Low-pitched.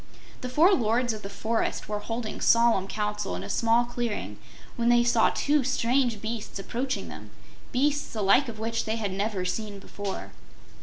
No: high, 230 Hz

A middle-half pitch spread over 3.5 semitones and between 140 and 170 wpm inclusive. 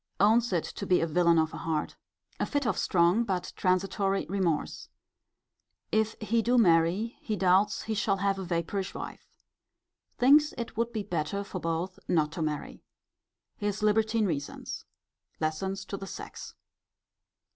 Yes: average, 4.2 semitones; average, 155 wpm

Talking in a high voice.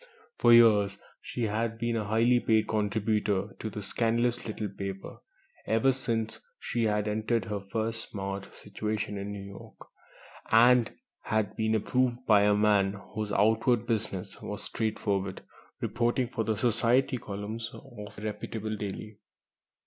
No: low, 110 Hz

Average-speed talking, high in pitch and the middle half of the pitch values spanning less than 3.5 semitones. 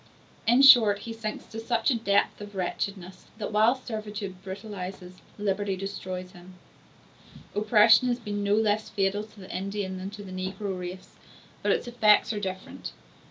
Yes: average, 160 wpm; high, 205 Hz; narrow, 2.5 semitones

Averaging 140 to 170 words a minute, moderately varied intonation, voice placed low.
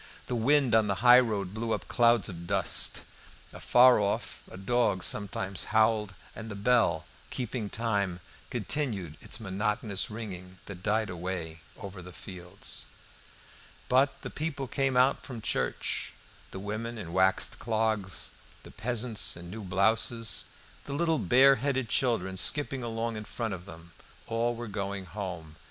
Yes: average, 145 wpm; average, 4.0 semitones; low, 110 Hz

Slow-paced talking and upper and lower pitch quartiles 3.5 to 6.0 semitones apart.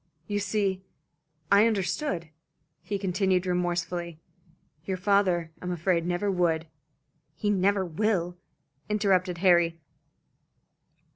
No: slow, 100 wpm; narrow, 2.6 semitones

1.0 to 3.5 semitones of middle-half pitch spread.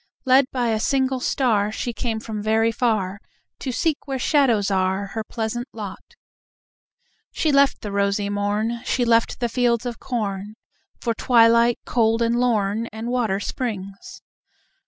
Yes: average, 2.9 semitones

